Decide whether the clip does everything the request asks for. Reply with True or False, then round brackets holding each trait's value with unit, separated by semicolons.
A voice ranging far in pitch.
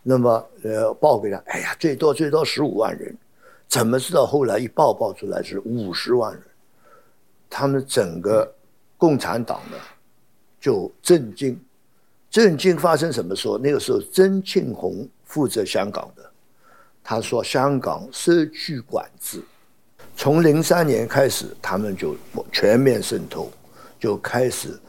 True (6.7 semitones)